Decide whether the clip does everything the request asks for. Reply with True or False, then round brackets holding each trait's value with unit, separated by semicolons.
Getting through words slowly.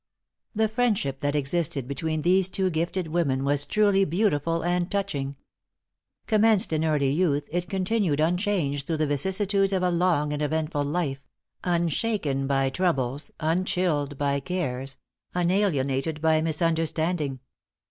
True (130 wpm)